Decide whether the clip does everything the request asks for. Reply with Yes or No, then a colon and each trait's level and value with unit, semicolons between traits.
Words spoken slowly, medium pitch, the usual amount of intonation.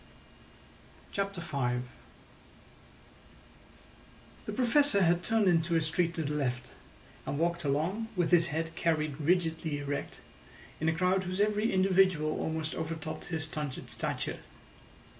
Yes: slow, 125 wpm; medium, 165 Hz; average, 3.3 semitones